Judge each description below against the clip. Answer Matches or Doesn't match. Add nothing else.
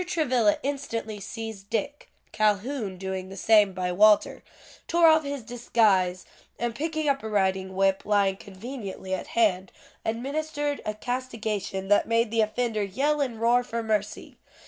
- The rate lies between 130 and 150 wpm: Matches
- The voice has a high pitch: Matches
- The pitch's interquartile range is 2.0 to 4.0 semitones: Doesn't match